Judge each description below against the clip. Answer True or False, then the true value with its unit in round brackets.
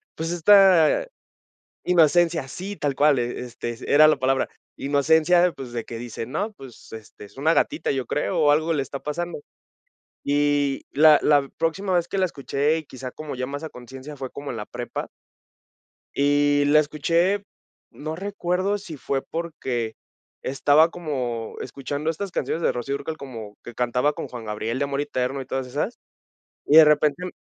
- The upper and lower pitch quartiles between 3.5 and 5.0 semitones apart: True (3.8 semitones)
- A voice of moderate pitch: True (145 Hz)